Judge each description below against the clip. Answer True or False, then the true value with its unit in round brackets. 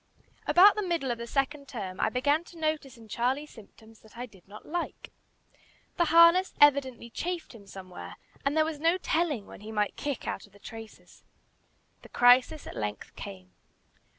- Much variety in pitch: True (6.3 semitones)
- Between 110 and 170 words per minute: False (180 wpm)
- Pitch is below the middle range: False (260 Hz)